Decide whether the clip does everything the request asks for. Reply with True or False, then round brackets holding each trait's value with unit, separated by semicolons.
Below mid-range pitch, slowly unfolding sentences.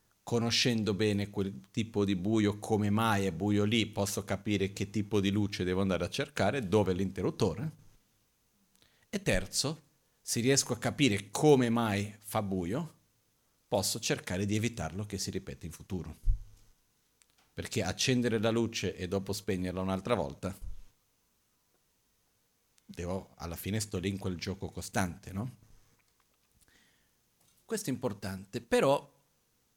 False (105 Hz; 135 wpm)